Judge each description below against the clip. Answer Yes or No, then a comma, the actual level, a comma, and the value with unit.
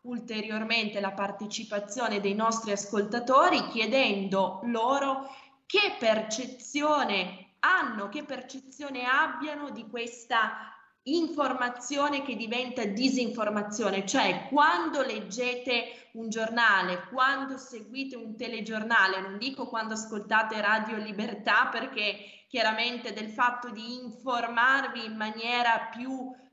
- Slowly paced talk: Yes, slow, 100 wpm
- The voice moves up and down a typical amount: Yes, average, 3.1 semitones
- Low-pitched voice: No, high, 235 Hz